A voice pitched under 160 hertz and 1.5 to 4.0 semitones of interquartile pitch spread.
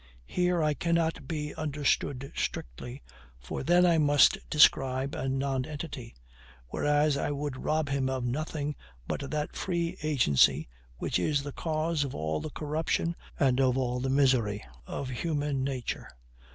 Yes: medium, 140 Hz; average, 2.9 semitones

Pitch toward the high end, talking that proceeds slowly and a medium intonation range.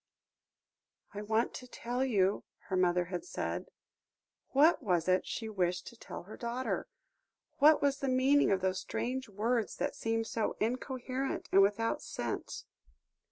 No: high, 225 Hz; average, 150 wpm; average, 5.0 semitones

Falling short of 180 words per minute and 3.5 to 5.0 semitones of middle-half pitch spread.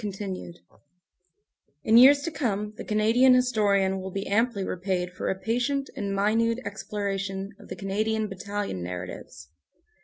No: average, 140 wpm; average, 2.8 semitones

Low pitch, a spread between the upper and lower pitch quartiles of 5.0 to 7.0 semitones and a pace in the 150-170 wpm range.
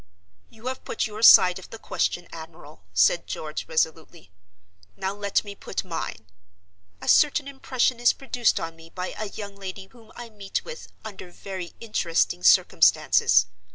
No: high, 195 Hz; wide, 5.4 semitones; average, 155 wpm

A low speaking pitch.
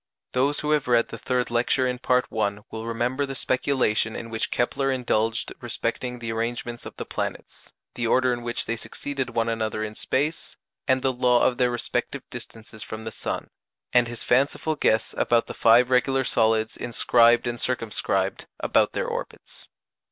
Yes: low, 120 Hz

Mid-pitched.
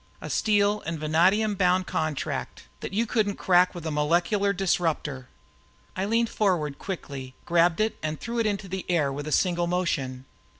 Yes: medium, 180 Hz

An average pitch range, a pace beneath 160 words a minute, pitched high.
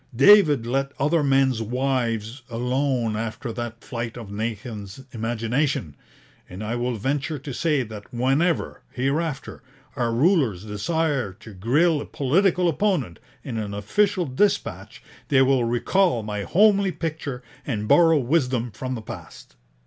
No: average, 5.0 semitones; slow, 135 wpm; low, 130 Hz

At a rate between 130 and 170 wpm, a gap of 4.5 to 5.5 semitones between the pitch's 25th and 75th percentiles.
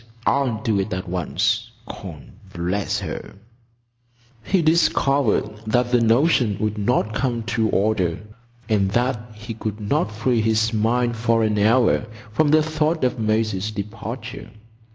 No: slow, 135 wpm; average, 2.7 semitones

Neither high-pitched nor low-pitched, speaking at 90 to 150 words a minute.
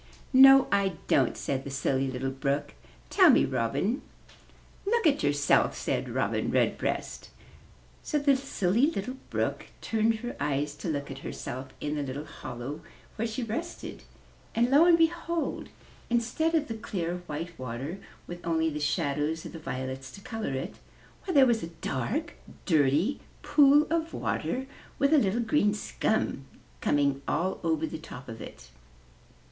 No: medium, 175 Hz; average, 160 wpm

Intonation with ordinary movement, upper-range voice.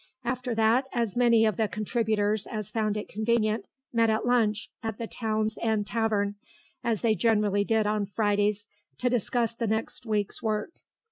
No: narrow, 1.6 semitones; high, 220 Hz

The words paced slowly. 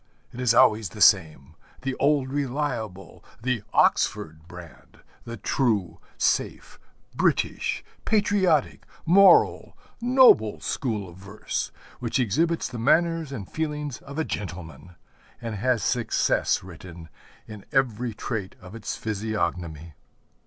Yes: slow, 115 wpm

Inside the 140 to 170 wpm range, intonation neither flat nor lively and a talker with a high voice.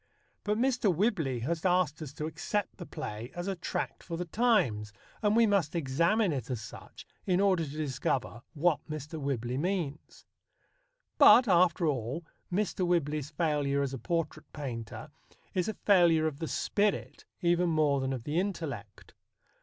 No: average, 160 wpm; average, 4.8 semitones; medium, 160 Hz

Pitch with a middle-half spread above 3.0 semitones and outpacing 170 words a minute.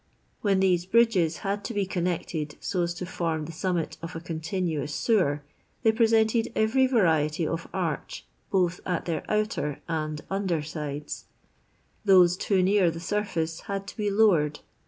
No: average, 4.0 semitones; average, 165 wpm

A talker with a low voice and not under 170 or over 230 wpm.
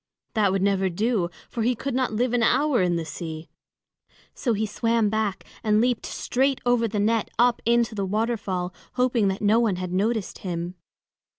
No: high, 220 Hz; average, 185 wpm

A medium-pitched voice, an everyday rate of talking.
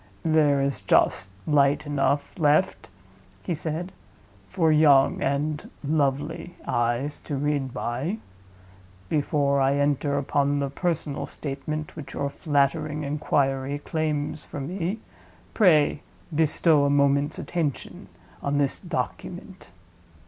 No: medium, 145 Hz; slow, 110 wpm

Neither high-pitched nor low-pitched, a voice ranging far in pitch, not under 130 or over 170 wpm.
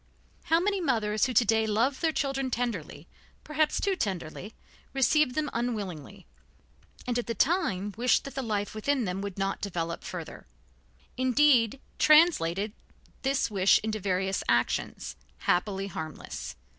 No: high, 220 Hz; wide, 5.8 semitones; average, 140 wpm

